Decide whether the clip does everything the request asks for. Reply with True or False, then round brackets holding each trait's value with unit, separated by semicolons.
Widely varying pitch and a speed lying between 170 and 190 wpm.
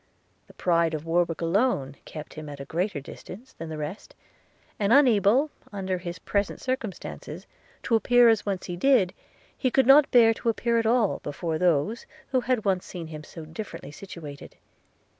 True (6.1 semitones; 175 wpm)